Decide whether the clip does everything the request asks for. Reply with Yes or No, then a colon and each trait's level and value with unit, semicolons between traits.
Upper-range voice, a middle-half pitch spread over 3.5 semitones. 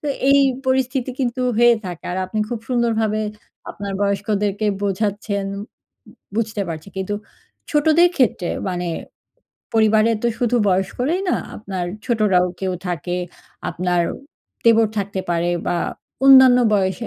Yes: high, 210 Hz; average, 4.1 semitones